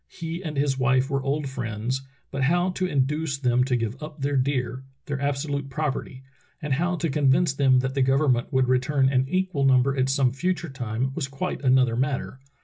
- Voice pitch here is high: No, low, 135 Hz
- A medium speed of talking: No, fast, 210 wpm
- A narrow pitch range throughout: Yes, narrow, 2.3 semitones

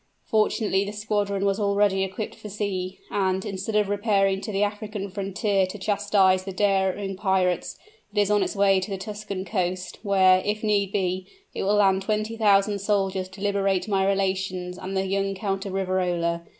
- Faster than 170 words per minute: Yes, average, 180 wpm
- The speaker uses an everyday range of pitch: No, narrow, 1.4 semitones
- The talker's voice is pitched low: No, high, 195 Hz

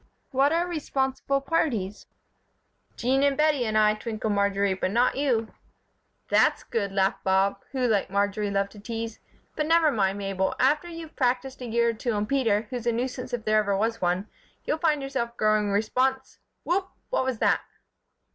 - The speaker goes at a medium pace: Yes, average, 175 wpm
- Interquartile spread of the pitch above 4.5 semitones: Yes, average, 4.9 semitones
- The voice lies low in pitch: No, high, 235 Hz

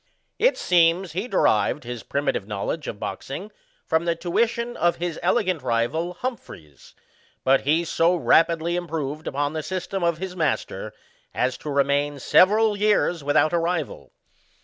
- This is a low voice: No, medium, 165 Hz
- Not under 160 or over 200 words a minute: No, average, 150 wpm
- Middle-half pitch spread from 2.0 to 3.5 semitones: No, average, 4.0 semitones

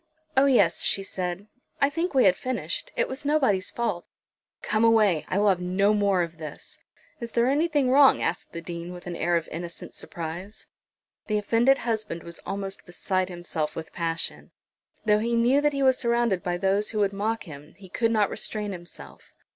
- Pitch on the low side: No, high, 200 Hz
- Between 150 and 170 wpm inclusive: No, average, 190 wpm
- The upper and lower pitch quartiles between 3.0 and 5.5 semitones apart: Yes, average, 5.1 semitones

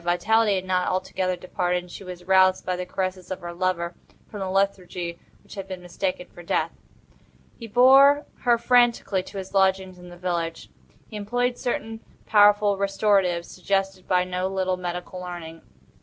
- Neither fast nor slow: Yes, average, 170 wpm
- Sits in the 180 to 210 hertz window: Yes, medium, 185 Hz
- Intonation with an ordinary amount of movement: No, narrow, 2.2 semitones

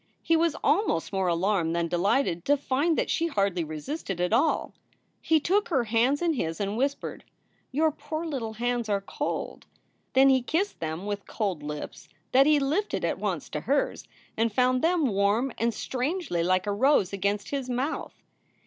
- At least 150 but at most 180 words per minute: Yes, average, 175 wpm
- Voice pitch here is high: Yes, high, 245 Hz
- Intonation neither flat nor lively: No, wide, 6.8 semitones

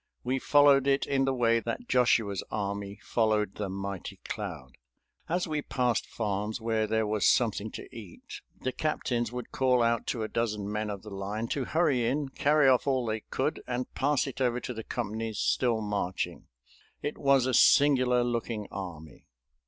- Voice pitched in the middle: No, low, 115 Hz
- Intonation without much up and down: No, average, 3.8 semitones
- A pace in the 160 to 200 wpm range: Yes, average, 175 wpm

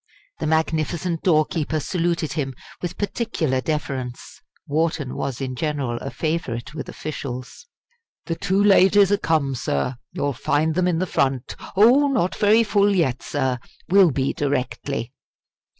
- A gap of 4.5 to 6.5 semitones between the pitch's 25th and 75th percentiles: Yes, average, 5.2 semitones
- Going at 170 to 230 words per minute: No, average, 140 wpm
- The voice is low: No, medium, 155 Hz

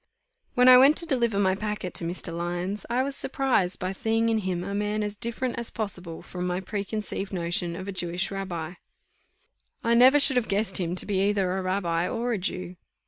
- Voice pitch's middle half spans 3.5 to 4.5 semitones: Yes, average, 4.1 semitones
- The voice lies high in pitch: Yes, high, 200 Hz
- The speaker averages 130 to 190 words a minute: No, fast, 205 wpm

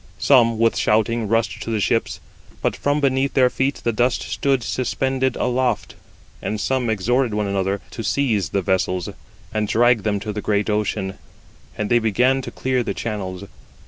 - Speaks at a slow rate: No, average, 175 wpm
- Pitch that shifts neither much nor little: Yes, average, 3.6 semitones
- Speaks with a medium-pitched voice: No, low, 115 Hz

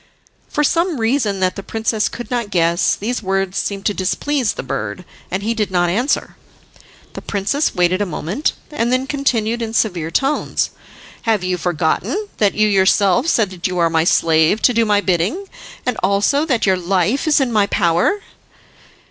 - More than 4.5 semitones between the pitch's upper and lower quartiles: Yes, average, 5.1 semitones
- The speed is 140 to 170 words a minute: No, average, 180 wpm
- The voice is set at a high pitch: Yes, high, 205 Hz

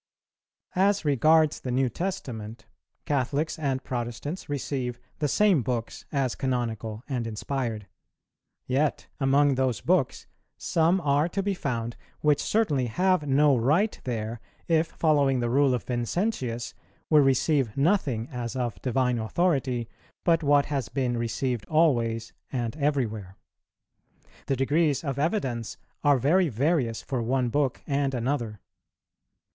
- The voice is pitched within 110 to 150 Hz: Yes, low, 135 Hz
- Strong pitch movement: No, average, 4.0 semitones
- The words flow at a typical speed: No, slow, 130 wpm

